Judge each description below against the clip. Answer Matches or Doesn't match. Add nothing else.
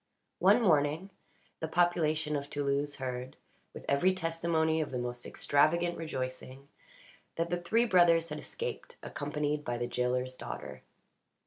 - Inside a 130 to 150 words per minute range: Matches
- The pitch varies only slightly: Doesn't match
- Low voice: Doesn't match